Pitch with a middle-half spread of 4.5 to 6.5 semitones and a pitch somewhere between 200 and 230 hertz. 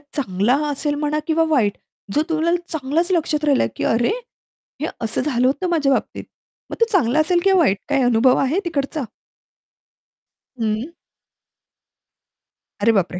No: average, 4.9 semitones; very high, 285 Hz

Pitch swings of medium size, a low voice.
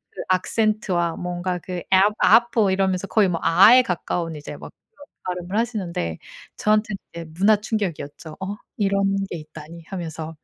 No: average, 3.8 semitones; medium, 185 Hz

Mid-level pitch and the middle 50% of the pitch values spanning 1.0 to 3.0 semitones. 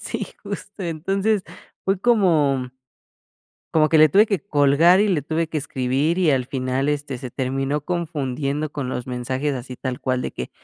No: medium, 145 Hz; average, 4.6 semitones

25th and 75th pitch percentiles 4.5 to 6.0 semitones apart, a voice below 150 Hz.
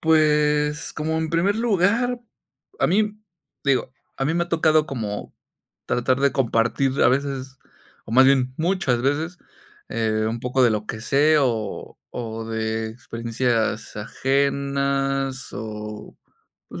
Yes: average, 5.1 semitones; low, 135 Hz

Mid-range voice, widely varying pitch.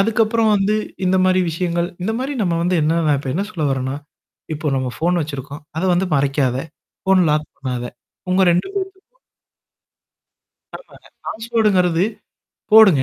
Yes: medium, 180 Hz; wide, 6.0 semitones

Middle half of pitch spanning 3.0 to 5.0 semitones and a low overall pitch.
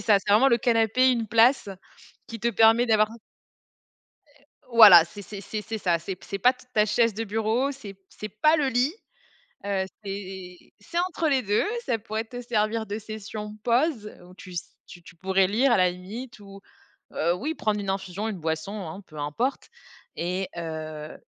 No: average, 3.6 semitones; high, 210 Hz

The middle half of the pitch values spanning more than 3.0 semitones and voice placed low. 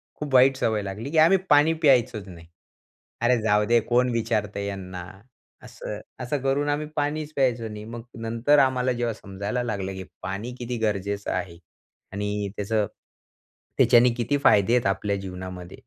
Yes: average, 4.2 semitones; low, 115 Hz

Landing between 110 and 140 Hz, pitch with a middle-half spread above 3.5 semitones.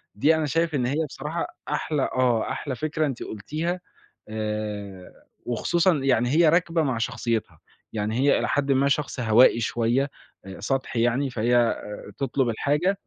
Yes: low, 135 Hz; average, 4.7 semitones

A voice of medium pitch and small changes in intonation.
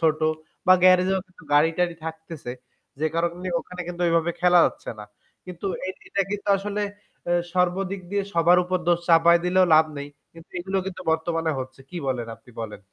Yes: medium, 175 Hz; narrow, 2.3 semitones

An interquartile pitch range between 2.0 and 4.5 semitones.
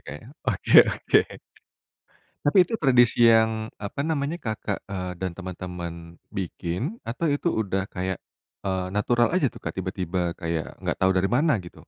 No: average, 5.0 semitones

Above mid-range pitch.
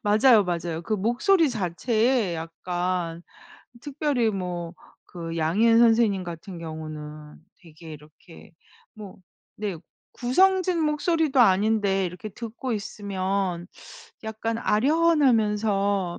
Yes: high, 205 Hz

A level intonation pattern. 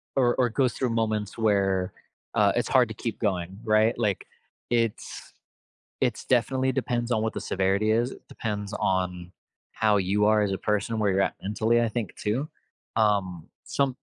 No: average, 3.2 semitones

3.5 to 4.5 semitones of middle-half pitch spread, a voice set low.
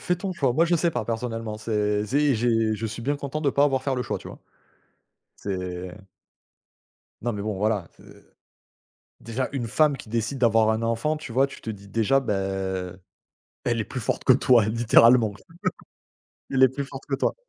Yes: average, 3.9 semitones; low, 120 Hz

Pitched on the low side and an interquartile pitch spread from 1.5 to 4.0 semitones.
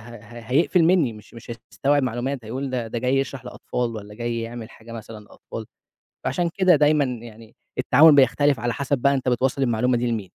Yes: low, 125 Hz; average, 3.3 semitones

